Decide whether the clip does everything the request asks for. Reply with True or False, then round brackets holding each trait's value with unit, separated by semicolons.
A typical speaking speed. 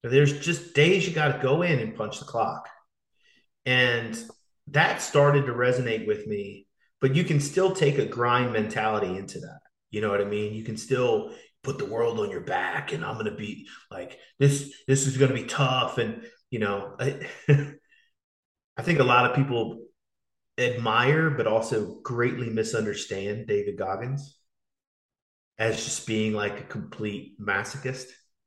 True (170 wpm)